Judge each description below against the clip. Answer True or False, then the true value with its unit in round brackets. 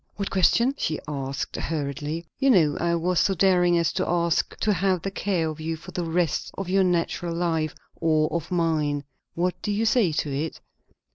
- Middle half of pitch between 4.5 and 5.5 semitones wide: False (2.8 semitones)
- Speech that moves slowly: False (195 wpm)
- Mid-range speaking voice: True (170 Hz)